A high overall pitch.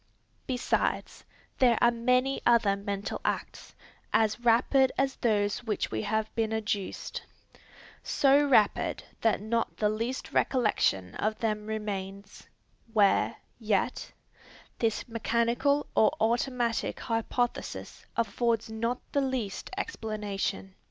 Yes: high, 225 Hz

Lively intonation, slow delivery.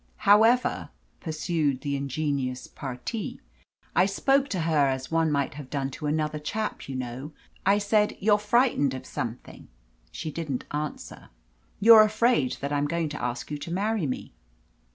No: wide, 6.8 semitones; average, 155 wpm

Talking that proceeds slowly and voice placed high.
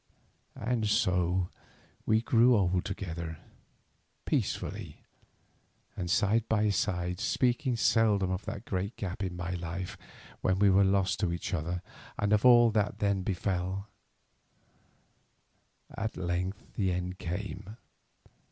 No: slow, 125 wpm; very low, 95 Hz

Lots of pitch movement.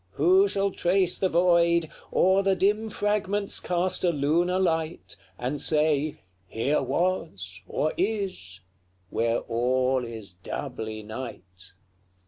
Yes: wide, 7.6 semitones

